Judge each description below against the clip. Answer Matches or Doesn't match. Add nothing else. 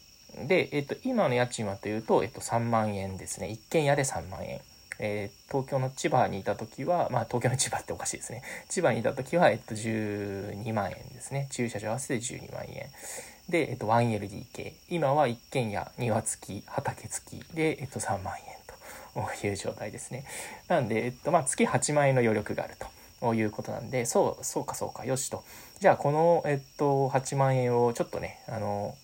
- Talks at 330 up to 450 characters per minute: Matches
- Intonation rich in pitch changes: Doesn't match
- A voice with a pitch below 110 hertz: Doesn't match